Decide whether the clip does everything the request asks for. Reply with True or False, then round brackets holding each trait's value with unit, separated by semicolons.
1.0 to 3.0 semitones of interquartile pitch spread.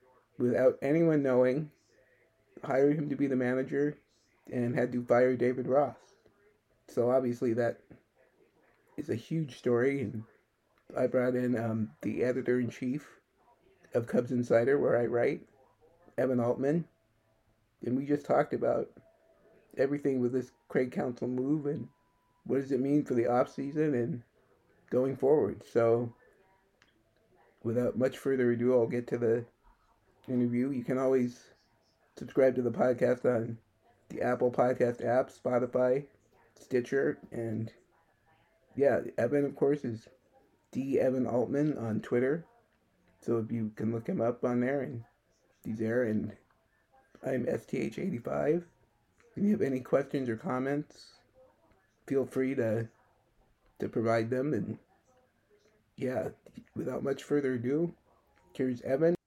True (2.4 semitones)